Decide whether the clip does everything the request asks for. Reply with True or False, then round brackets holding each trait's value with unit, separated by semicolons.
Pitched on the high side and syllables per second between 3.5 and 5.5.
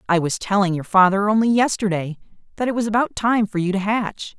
False (205 Hz; 5.8 syllables/s)